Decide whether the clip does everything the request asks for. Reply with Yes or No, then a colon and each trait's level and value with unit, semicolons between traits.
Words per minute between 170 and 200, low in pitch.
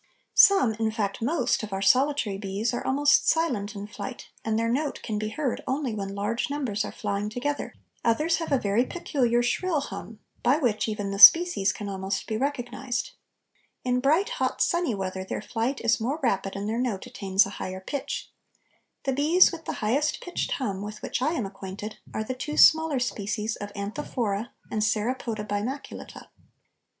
No: average, 180 wpm; high, 230 Hz